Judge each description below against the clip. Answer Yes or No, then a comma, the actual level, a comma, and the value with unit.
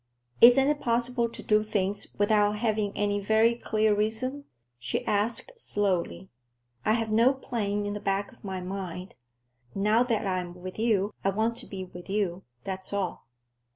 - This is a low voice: No, high, 210 Hz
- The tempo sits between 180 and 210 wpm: No, average, 165 wpm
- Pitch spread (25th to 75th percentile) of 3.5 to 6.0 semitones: No, average, 2.7 semitones